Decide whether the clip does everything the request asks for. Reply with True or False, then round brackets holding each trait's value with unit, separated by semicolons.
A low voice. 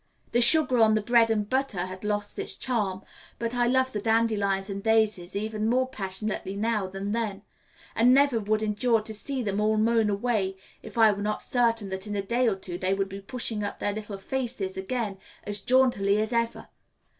False (215 Hz)